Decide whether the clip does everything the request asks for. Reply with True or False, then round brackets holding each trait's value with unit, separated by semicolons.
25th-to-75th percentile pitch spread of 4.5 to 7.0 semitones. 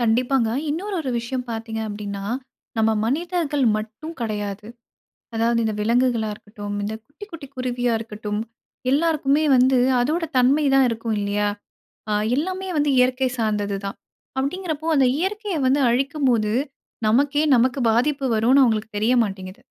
True (4.9 semitones)